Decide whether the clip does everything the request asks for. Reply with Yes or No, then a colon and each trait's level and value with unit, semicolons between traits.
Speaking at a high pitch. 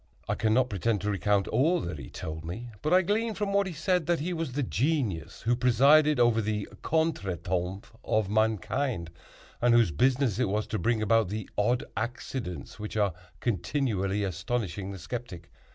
No: low, 110 Hz